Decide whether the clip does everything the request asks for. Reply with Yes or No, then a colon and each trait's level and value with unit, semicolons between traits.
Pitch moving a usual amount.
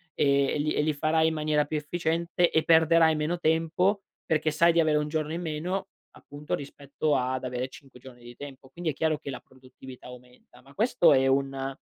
Yes: average, 3.2 semitones